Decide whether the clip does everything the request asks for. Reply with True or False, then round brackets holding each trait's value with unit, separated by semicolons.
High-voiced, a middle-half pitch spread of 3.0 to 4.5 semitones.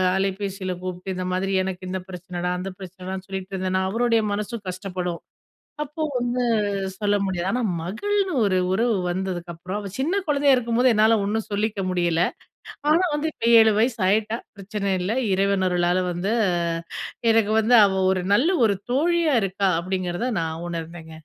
True (195 Hz; 3.7 semitones)